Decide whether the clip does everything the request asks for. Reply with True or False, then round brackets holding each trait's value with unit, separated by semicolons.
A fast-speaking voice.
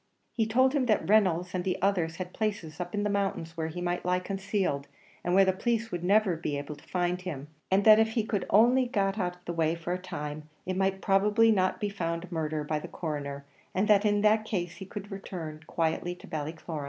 True (225 wpm)